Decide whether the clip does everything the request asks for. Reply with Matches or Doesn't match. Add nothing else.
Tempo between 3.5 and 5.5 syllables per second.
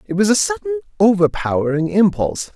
Doesn't match